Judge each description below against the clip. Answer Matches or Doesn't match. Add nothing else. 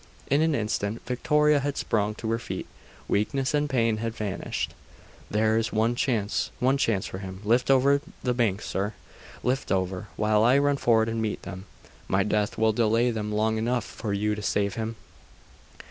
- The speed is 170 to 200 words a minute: Matches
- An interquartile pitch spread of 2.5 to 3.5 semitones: Matches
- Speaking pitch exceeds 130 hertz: Doesn't match